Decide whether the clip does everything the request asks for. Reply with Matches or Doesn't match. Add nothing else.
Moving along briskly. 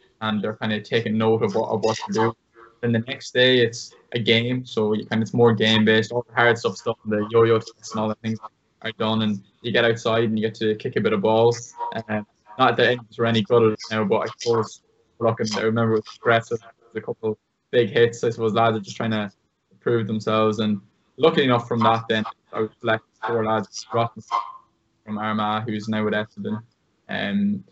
Matches